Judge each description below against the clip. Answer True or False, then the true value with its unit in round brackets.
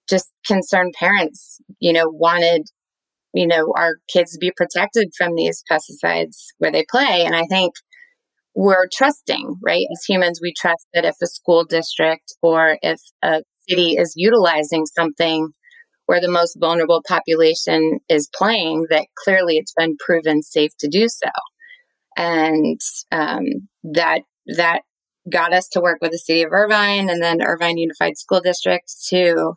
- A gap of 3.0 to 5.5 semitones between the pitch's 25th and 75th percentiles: False (2.6 semitones)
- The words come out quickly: False (155 wpm)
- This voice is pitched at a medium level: True (170 Hz)